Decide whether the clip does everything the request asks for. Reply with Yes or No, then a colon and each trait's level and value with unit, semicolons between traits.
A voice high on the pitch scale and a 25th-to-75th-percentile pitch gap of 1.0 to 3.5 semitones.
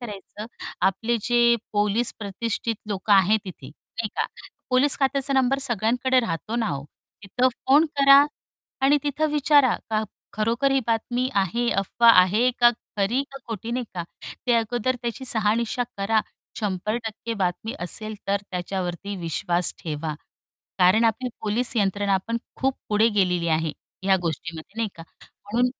No: high, 220 Hz; average, 4.0 semitones